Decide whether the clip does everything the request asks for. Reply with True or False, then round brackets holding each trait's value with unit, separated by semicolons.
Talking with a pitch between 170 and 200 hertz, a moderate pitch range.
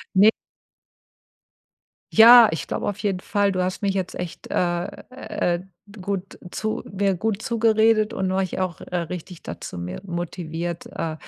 True (190 Hz; 3.3 semitones)